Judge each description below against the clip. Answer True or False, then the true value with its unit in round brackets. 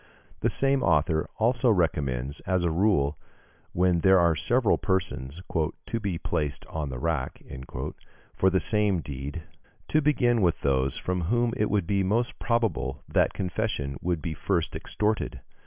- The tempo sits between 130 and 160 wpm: True (155 wpm)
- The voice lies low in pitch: True (90 Hz)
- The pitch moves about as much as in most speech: False (5.8 semitones)